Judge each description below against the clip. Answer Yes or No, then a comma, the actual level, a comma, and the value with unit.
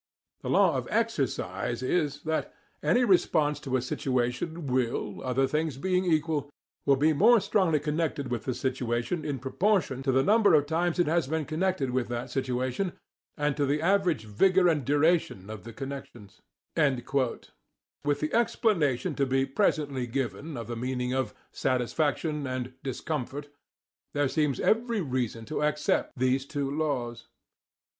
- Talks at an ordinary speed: Yes, average, 150 wpm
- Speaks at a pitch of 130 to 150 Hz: Yes, medium, 140 Hz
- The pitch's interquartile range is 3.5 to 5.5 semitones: Yes, average, 3.9 semitones